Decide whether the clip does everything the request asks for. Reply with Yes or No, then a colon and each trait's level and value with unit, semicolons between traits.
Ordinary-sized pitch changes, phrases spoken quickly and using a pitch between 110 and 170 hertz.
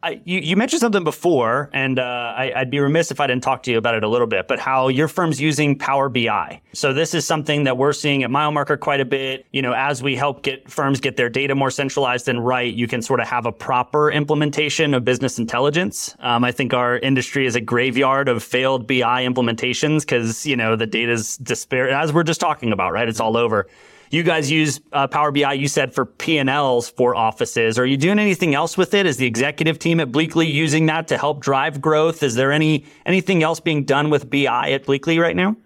Yes: average, 3.5 semitones; fast, 235 wpm; medium, 140 Hz